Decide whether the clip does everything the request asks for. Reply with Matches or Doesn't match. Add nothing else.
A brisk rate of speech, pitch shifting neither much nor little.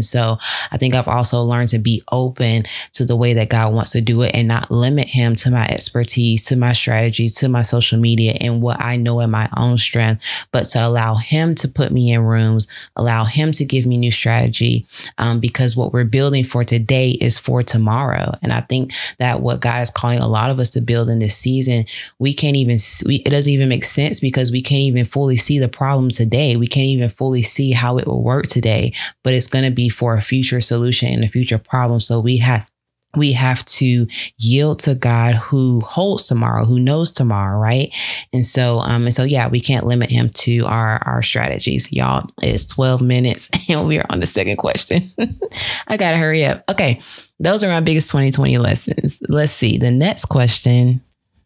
Doesn't match